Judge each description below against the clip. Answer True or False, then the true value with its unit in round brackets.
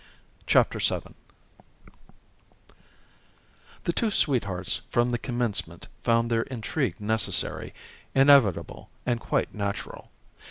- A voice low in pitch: True (115 Hz)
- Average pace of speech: False (90 wpm)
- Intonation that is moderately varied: True (3.6 semitones)